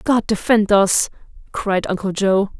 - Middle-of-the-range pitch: No, high, 200 Hz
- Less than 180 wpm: Yes, average, 140 wpm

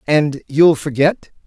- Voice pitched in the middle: Yes, medium, 150 Hz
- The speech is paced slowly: Yes, slow, 125 wpm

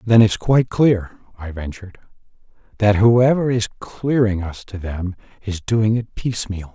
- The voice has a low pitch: Yes, low, 105 Hz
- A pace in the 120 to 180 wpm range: Yes, average, 150 wpm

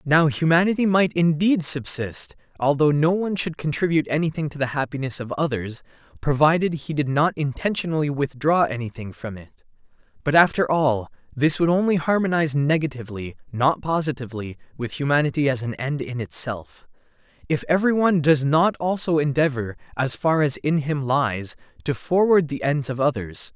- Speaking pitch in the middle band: Yes, medium, 145 Hz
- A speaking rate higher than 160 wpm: No, average, 155 wpm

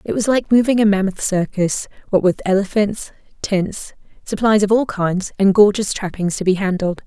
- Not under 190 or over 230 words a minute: No, average, 180 wpm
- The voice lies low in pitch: No, high, 200 Hz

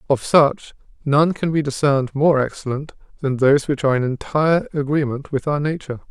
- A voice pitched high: No, medium, 140 Hz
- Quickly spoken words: No, average, 175 wpm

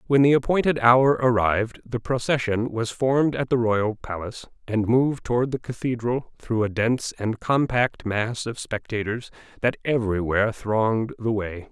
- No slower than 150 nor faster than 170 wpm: Yes, average, 165 wpm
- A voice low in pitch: Yes, low, 115 Hz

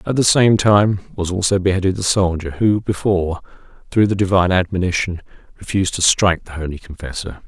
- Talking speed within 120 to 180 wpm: Yes, average, 170 wpm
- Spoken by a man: Yes, male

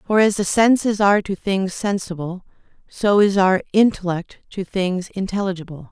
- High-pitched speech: Yes, high, 195 Hz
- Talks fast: No, average, 150 wpm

